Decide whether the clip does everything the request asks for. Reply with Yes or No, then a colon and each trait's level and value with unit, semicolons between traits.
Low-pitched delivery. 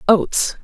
No: high, 200 Hz